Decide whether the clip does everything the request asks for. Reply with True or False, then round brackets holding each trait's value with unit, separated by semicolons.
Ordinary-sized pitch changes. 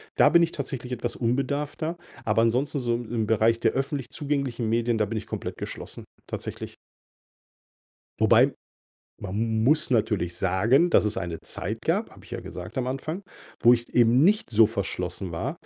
True (3.7 semitones)